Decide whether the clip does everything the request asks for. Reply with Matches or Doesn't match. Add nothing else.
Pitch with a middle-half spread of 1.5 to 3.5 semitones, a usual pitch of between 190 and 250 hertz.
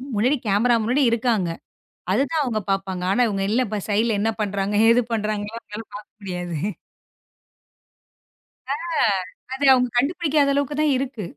Doesn't match